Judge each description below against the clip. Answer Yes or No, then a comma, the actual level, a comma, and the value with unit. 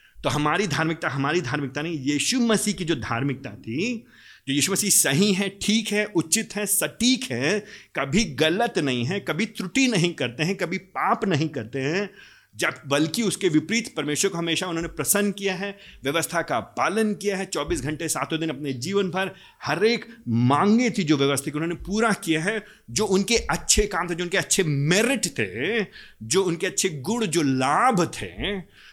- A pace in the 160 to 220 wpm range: Yes, average, 185 wpm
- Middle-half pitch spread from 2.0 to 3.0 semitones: No, wide, 5.4 semitones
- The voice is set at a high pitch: No, medium, 180 Hz